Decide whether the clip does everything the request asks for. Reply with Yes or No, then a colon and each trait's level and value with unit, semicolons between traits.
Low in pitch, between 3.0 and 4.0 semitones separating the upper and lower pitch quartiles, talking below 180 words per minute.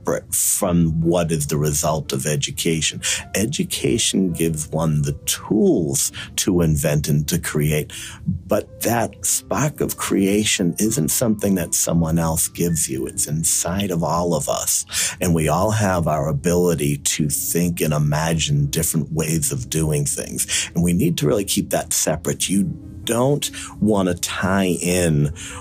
Yes: very low, 85 Hz; average, 3.6 semitones; average, 150 wpm